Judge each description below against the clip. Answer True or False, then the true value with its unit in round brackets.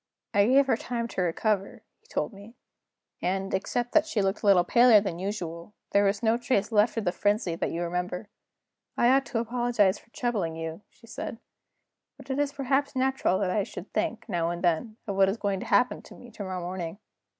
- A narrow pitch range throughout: False (4.6 semitones)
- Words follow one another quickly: True (210 wpm)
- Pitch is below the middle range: False (205 Hz)